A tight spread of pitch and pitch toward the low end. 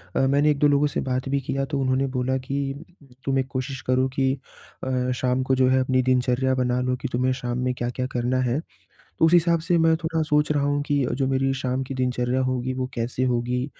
Yes: narrow, 1.6 semitones; low, 130 Hz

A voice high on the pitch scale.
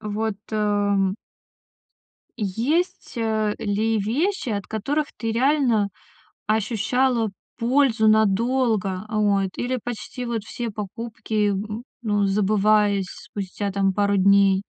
Yes: high, 215 Hz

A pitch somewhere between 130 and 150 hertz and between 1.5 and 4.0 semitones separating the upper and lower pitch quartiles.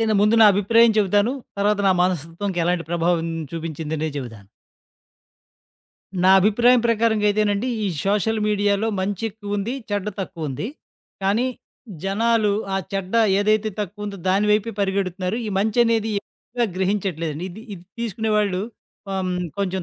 No: high, 200 Hz; average, 2.9 semitones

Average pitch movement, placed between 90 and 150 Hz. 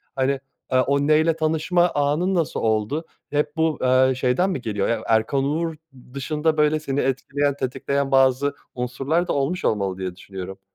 Yes: average, 3.4 semitones; medium, 140 Hz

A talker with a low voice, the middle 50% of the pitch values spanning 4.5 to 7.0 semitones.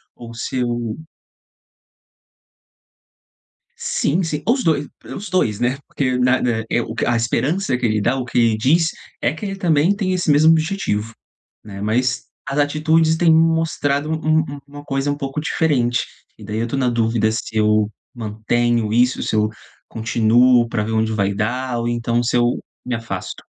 Yes: low, 125 Hz; average, 5.1 semitones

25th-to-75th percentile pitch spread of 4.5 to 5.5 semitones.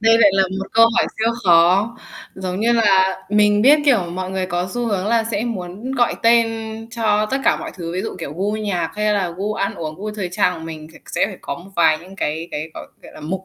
No: average, 3.8 semitones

